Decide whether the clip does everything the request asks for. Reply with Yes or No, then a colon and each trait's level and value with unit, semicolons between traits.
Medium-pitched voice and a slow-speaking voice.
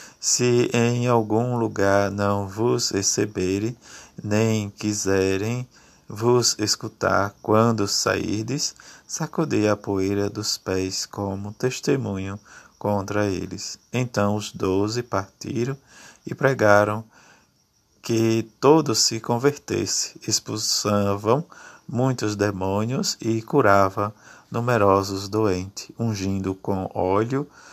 No: low, 110 Hz; slow, 90 wpm